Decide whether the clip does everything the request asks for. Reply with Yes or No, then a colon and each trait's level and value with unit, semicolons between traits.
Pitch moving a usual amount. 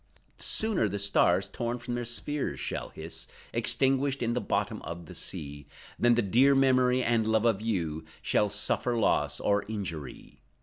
Yes: average, 4.1 semitones